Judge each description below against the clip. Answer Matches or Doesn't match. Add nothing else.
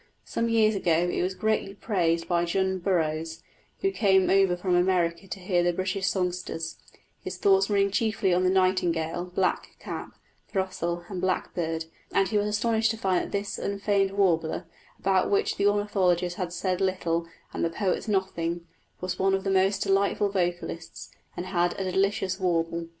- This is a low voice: Doesn't match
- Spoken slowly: Doesn't match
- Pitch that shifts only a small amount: Matches